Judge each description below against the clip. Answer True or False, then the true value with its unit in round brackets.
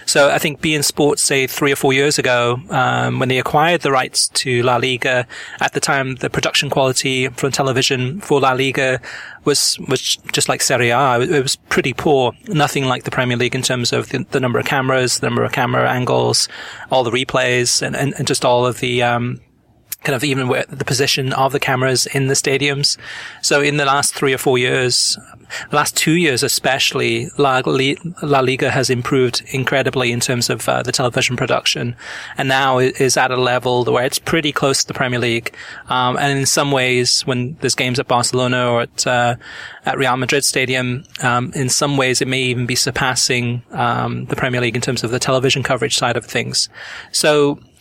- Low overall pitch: True (130 Hz)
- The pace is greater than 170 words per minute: True (205 wpm)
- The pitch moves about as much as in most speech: False (2.1 semitones)